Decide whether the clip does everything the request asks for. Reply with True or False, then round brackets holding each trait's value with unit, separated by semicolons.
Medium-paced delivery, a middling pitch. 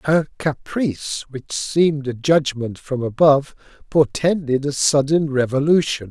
False (120 wpm; 145 Hz)